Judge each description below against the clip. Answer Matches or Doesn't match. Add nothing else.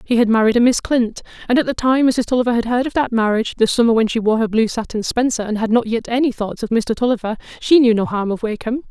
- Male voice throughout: Doesn't match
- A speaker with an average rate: Doesn't match